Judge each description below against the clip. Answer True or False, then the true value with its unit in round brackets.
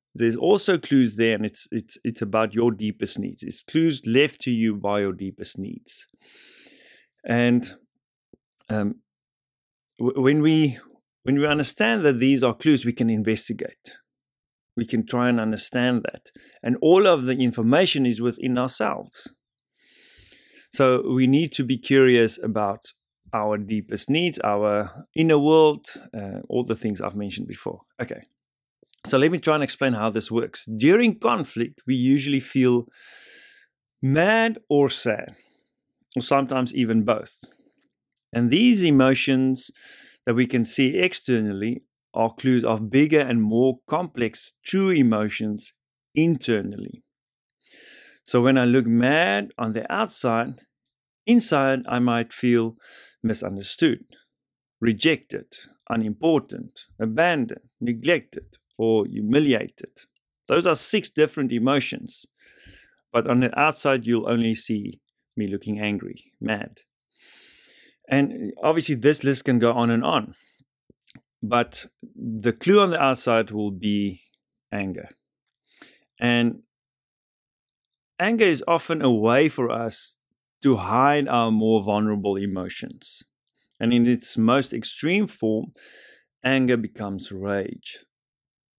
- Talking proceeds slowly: True (125 wpm)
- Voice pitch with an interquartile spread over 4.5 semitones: False (3.7 semitones)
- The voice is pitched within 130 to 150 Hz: False (120 Hz)